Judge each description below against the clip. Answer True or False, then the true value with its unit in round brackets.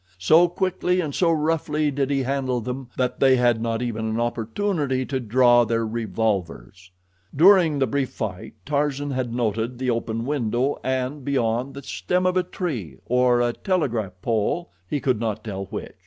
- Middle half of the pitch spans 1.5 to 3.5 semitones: False (4.2 semitones)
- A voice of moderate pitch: False (125 Hz)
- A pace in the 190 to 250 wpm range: False (170 wpm)